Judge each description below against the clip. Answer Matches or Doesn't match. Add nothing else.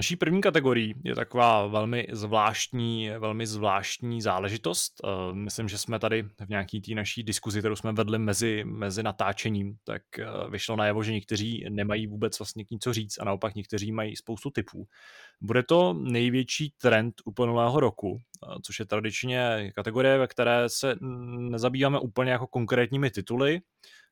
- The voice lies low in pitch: Matches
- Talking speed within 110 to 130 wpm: Doesn't match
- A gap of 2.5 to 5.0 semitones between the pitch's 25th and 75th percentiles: Matches